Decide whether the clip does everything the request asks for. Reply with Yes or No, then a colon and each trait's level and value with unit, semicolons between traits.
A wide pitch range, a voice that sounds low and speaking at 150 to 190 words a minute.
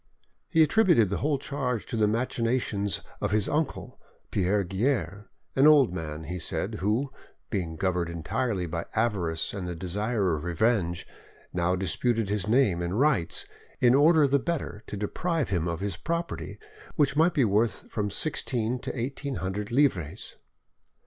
Yes: wide, 6.7 semitones; low, 105 Hz; average, 155 wpm